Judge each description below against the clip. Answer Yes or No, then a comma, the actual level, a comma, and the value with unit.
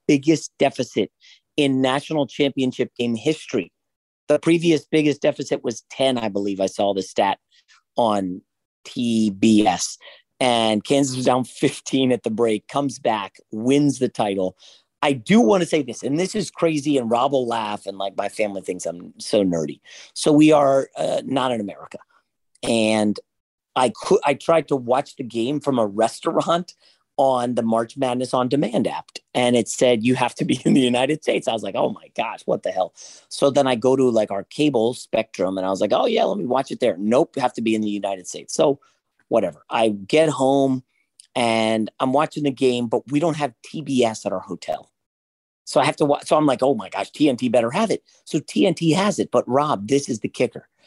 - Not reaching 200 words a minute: No, fast, 205 wpm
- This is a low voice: Yes, low, 130 Hz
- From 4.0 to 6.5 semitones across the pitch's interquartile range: Yes, average, 4.3 semitones